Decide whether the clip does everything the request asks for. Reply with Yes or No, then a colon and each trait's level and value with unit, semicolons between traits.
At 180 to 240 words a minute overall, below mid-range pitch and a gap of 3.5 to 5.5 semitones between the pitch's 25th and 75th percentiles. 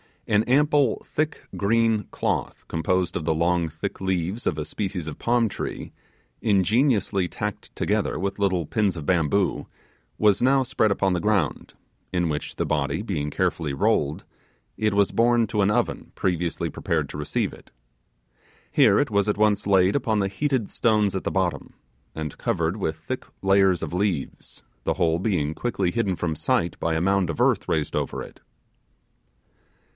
No: average, 170 wpm; very low, 95 Hz; average, 4.4 semitones